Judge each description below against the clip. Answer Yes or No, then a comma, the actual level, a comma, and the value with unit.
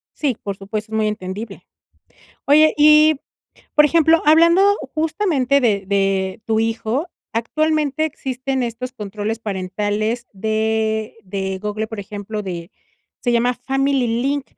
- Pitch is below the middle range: No, high, 225 Hz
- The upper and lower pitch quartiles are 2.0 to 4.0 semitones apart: No, average, 5.2 semitones